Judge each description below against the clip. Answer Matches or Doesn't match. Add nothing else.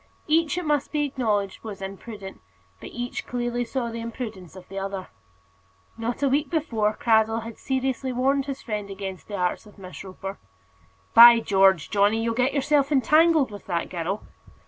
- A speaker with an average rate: Matches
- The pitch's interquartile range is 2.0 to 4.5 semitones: Doesn't match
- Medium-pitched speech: Doesn't match